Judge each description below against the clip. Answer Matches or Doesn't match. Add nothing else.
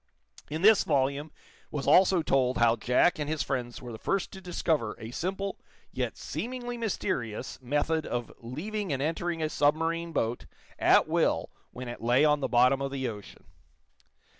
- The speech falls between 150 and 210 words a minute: Matches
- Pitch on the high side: Doesn't match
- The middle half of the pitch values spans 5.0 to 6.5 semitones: Matches